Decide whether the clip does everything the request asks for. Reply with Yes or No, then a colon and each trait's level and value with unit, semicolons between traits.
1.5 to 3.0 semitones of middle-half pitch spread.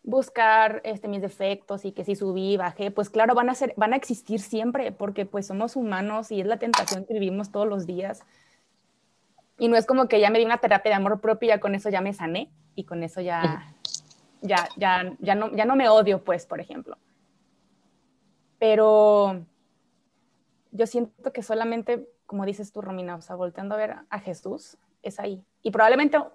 Yes: average, 2.7 semitones